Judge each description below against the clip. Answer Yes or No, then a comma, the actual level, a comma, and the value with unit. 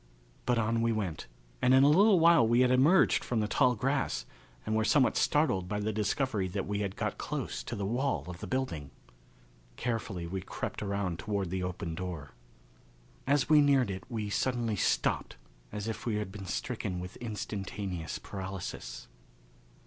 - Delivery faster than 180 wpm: No, average, 175 wpm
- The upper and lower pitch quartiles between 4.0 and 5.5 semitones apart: Yes, average, 5.0 semitones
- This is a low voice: Yes, low, 105 Hz